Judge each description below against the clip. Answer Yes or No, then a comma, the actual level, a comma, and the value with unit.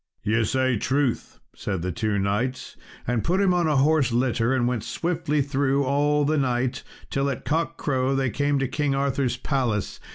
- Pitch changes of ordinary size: Yes, average, 3.0 semitones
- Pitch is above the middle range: No, low, 135 Hz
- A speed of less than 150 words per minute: No, average, 185 wpm